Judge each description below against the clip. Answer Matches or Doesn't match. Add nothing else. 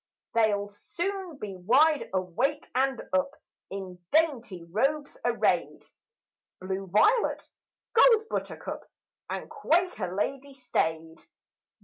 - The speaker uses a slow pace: Matches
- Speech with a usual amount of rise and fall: Doesn't match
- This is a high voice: Matches